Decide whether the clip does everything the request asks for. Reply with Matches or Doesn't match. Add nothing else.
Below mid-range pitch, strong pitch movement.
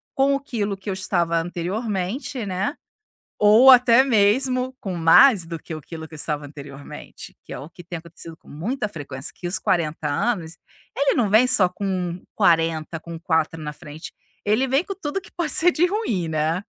Doesn't match